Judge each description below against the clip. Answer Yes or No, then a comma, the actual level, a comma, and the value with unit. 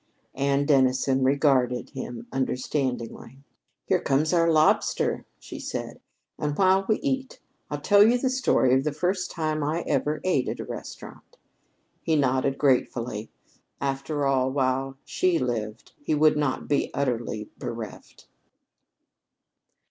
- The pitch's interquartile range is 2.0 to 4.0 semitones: Yes, average, 3.3 semitones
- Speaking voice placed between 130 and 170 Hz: Yes, medium, 140 Hz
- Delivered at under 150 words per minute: Yes, slow, 135 wpm